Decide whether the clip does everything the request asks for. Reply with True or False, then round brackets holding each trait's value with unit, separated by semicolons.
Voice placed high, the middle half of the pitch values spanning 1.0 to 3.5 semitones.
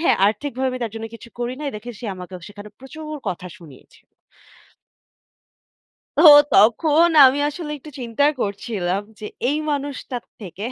False (240 Hz; 5.6 semitones)